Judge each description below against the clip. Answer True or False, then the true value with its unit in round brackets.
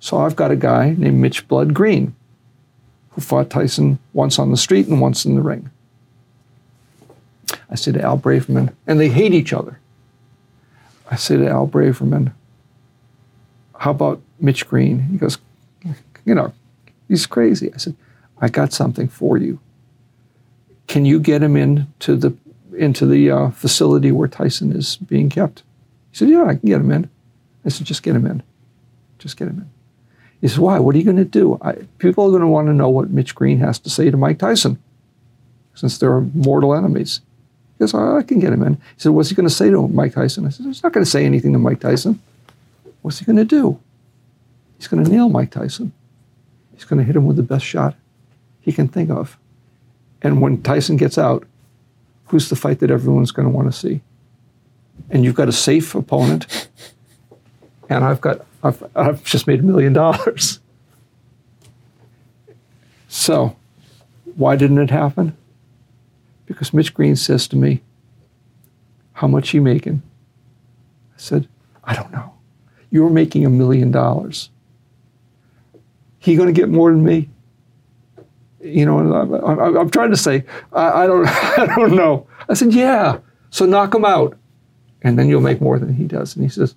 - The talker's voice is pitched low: True (125 Hz)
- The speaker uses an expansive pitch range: False (3.3 semitones)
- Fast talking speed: False (185 wpm)